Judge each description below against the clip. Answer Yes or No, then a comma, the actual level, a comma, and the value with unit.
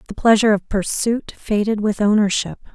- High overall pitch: Yes, high, 210 Hz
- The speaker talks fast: No, average, 155 wpm